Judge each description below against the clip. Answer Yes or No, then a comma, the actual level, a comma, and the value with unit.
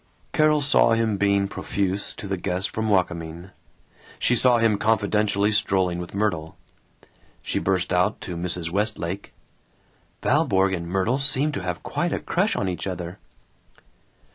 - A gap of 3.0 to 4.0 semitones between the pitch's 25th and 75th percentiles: Yes, average, 3.3 semitones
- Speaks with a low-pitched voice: Yes, low, 100 Hz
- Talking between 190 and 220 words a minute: No, average, 145 wpm